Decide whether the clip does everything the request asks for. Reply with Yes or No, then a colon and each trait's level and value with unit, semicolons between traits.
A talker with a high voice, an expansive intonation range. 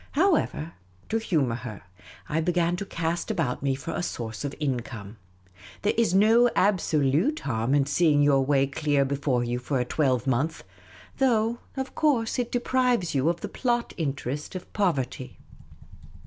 No: medium, 155 Hz; wide, 7.6 semitones